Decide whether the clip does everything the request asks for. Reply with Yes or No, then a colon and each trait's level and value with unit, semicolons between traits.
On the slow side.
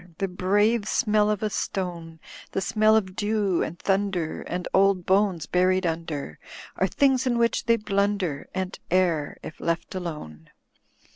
No: average, 150 wpm